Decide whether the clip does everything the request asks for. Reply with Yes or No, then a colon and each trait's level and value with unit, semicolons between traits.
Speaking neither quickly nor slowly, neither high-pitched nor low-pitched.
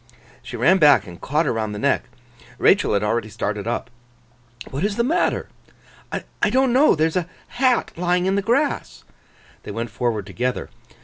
Yes: average, 180 wpm; medium, 155 Hz